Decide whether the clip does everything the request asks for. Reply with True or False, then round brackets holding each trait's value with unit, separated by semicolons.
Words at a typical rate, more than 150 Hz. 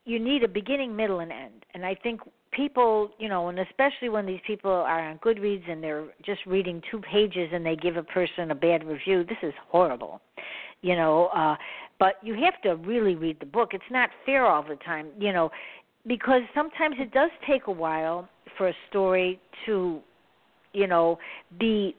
True (195 wpm; 190 Hz)